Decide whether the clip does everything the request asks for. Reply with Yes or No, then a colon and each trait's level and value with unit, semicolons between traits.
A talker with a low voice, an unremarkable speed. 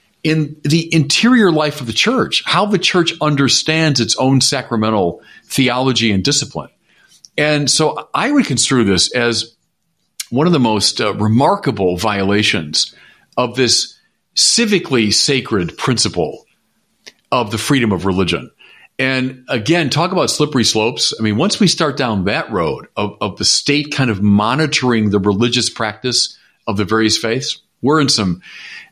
Yes: low, 130 Hz; average, 150 wpm